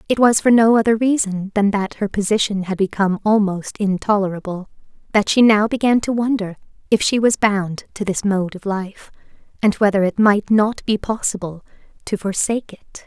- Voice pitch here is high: Yes, high, 205 Hz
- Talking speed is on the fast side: No, average, 180 wpm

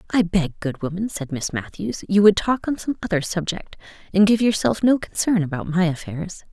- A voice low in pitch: No, medium, 185 Hz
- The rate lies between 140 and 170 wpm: No, average, 200 wpm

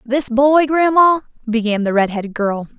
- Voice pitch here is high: Yes, very high, 250 Hz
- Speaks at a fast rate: No, average, 175 wpm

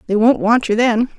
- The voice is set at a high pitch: Yes, high, 230 Hz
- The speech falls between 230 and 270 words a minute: Yes, fast, 255 wpm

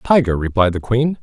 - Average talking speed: Yes, average, 195 wpm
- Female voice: No, male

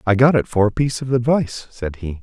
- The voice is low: Yes, low, 115 Hz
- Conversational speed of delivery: No, fast, 270 wpm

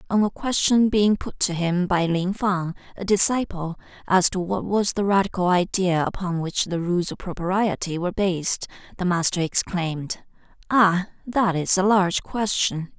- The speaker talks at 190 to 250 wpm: No, average, 165 wpm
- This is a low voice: No, medium, 185 Hz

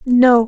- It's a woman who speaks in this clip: Yes, female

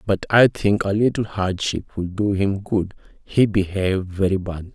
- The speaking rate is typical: Yes, average, 175 wpm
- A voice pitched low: Yes, low, 100 Hz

